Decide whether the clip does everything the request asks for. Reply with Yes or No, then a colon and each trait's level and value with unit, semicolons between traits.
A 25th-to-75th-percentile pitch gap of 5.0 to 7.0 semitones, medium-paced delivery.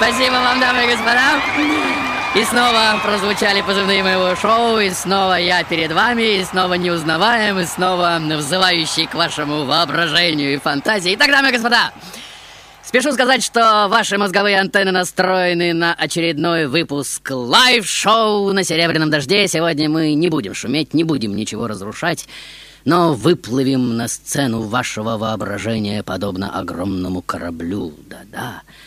Yes: wide, 5.5 semitones; average, 135 wpm